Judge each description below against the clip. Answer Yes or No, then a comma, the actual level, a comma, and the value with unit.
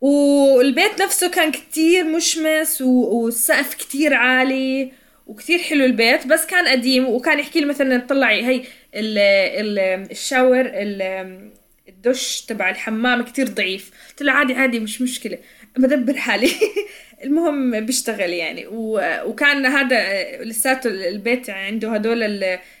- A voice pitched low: No, very high, 255 Hz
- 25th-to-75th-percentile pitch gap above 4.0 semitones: Yes, average, 4.6 semitones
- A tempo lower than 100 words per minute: No, average, 125 wpm